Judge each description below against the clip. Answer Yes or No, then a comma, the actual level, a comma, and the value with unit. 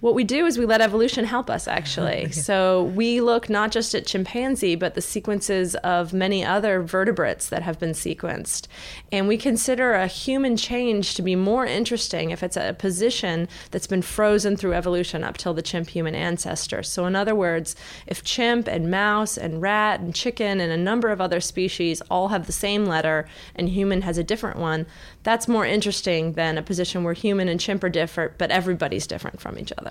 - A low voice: No, high, 190 Hz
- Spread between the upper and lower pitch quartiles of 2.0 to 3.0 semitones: No, average, 3.9 semitones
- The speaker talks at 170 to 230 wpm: Yes, average, 200 wpm